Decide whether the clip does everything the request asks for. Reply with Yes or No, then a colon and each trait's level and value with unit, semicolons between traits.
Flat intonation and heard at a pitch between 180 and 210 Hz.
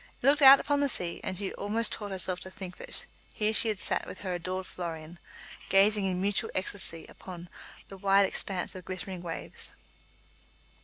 Yes: narrow, 2.2 semitones; high, 190 Hz